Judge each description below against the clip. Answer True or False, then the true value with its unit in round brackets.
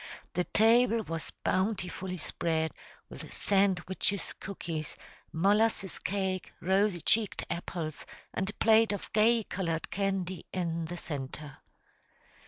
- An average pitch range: True (3.4 semitones)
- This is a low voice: False (190 Hz)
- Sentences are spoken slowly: True (110 wpm)